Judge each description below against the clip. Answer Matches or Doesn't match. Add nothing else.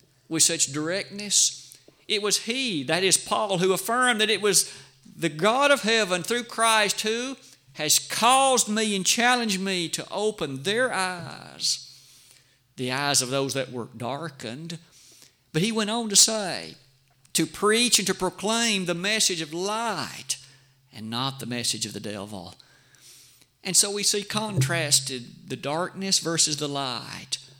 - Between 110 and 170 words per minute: Matches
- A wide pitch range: Matches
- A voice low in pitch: Doesn't match